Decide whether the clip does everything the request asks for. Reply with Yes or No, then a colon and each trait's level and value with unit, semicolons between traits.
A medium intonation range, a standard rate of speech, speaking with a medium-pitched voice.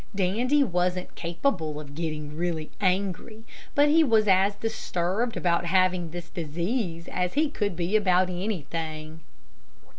No: average, 4.1 semitones; slow, 130 wpm; medium, 180 Hz